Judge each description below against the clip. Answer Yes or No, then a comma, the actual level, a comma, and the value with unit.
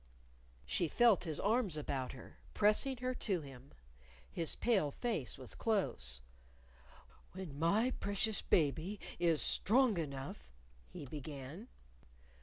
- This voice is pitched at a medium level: Yes, medium, 165 Hz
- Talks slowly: Yes, slow, 120 wpm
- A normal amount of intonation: No, wide, 7.5 semitones